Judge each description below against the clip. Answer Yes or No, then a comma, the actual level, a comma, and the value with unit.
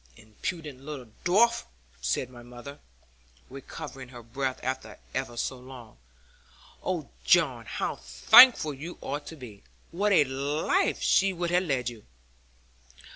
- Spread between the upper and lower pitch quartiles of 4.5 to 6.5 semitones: Yes, wide, 5.4 semitones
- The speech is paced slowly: Yes, slow, 130 wpm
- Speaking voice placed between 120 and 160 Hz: Yes, low, 135 Hz